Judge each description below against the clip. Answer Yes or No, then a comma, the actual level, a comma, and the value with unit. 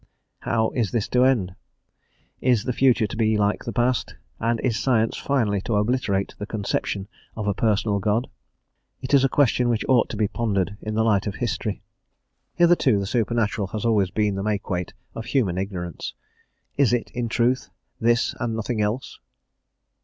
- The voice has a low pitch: Yes, low, 110 Hz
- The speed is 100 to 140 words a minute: No, average, 175 wpm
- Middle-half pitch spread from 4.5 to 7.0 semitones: No, average, 2.9 semitones